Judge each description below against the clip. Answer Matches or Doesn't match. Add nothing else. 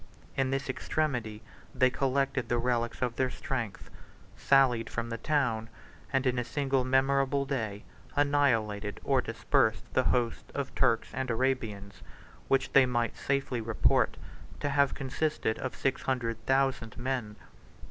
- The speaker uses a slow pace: Doesn't match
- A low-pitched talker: Matches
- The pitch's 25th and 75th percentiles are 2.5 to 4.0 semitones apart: Matches